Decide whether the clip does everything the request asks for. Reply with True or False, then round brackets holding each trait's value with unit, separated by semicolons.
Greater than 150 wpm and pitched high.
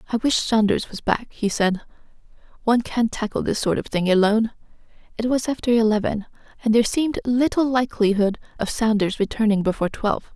True (170 wpm; 220 Hz)